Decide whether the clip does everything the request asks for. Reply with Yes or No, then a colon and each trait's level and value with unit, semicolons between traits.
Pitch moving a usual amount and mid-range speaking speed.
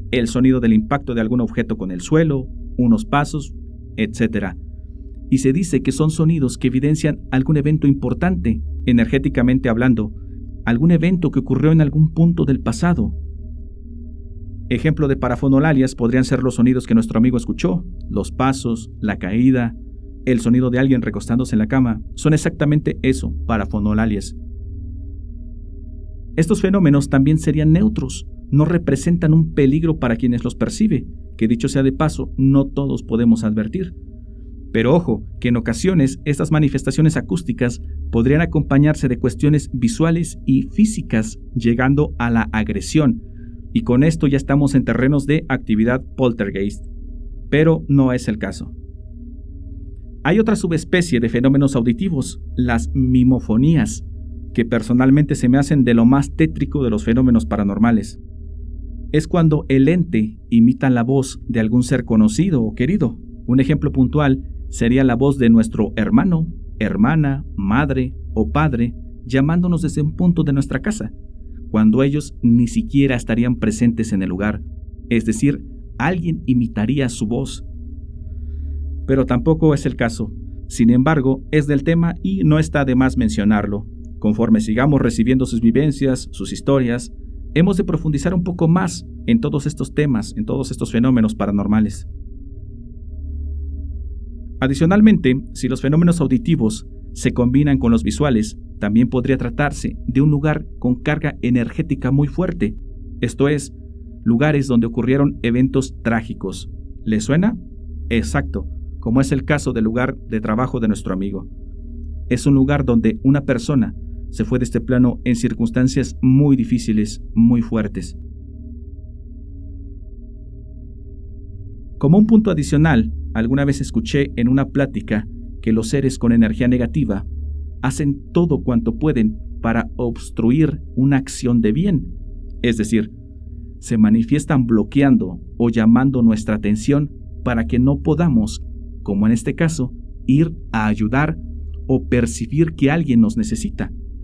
No: wide, 6.6 semitones; average, 140 wpm